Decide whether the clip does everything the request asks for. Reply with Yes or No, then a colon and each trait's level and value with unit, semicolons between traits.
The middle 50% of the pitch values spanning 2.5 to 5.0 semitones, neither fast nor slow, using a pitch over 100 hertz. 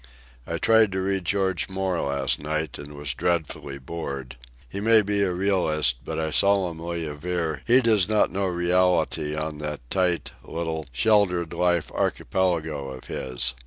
No: average, 4.1 semitones; average, 155 wpm; very low, 85 Hz